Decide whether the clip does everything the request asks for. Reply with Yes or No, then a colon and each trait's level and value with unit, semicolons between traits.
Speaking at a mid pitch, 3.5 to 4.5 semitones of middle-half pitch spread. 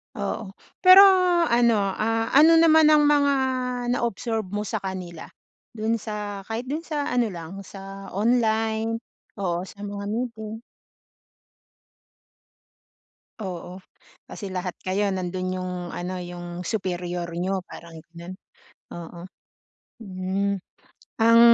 No: high, 200 Hz; average, 3.8 semitones